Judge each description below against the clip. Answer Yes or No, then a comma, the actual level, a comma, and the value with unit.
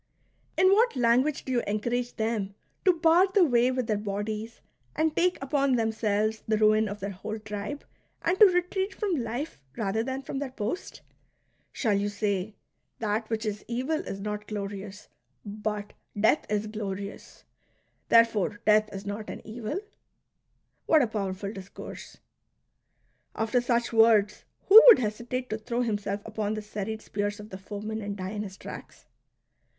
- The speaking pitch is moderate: No, high, 220 Hz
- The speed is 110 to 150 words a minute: No, average, 170 wpm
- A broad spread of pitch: No, average, 3.3 semitones